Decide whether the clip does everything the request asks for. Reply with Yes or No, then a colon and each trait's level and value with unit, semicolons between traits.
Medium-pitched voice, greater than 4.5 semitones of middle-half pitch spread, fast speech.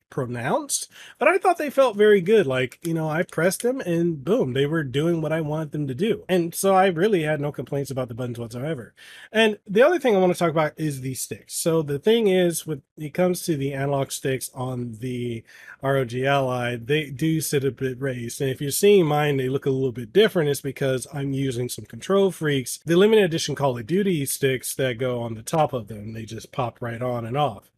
Yes: medium, 145 Hz; wide, 5.4 semitones; fast, 235 wpm